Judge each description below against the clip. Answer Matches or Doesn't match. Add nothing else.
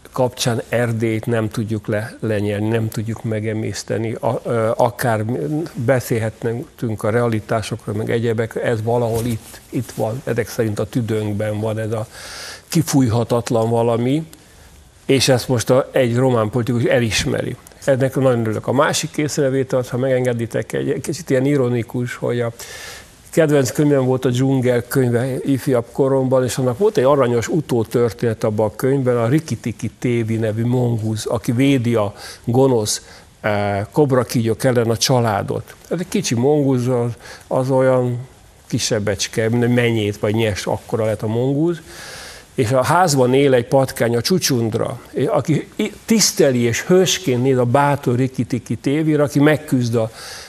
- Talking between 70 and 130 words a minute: Doesn't match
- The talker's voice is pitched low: Matches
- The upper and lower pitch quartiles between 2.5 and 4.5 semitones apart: Matches